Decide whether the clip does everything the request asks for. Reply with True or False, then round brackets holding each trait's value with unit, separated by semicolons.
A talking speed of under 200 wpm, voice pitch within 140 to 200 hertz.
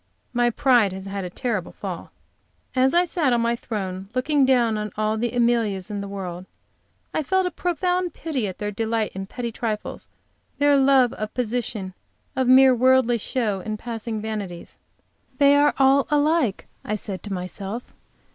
False (170 wpm; 235 Hz)